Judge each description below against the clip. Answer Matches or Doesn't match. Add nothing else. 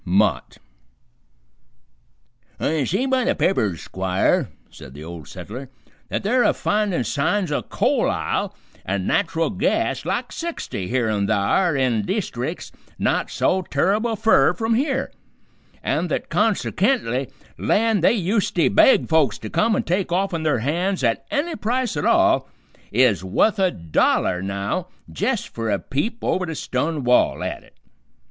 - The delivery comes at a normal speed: Matches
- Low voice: Doesn't match